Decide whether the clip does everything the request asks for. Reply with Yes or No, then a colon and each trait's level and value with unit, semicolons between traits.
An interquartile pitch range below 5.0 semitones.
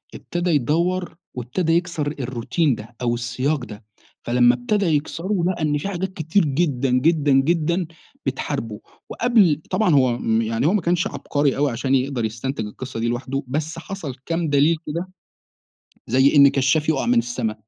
No: wide, 5.4 semitones